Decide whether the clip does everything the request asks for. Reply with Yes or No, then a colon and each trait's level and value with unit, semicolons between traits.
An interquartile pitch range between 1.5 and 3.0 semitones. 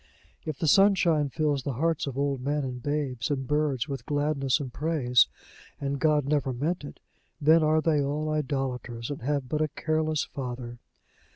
Yes: narrow, 2.6 semitones